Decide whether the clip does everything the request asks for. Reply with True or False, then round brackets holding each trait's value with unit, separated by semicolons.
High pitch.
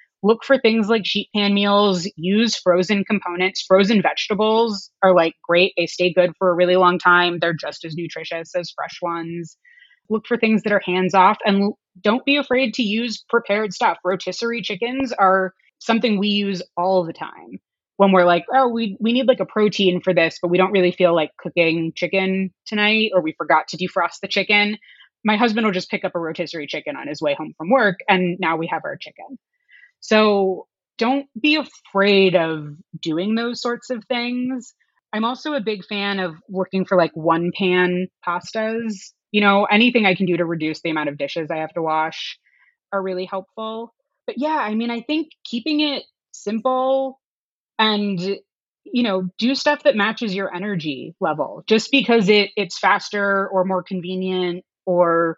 True (200 Hz)